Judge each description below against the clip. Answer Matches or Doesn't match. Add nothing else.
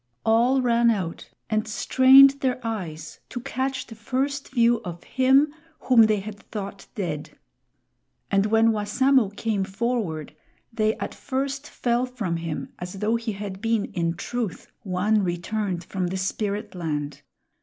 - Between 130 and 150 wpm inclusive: Matches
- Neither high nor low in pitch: Doesn't match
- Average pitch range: Matches